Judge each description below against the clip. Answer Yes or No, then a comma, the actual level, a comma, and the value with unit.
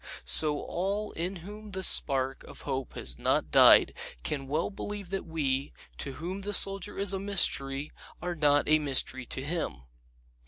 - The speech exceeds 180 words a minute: No, average, 165 wpm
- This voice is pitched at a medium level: Yes, medium, 160 Hz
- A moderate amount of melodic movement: No, wide, 6.1 semitones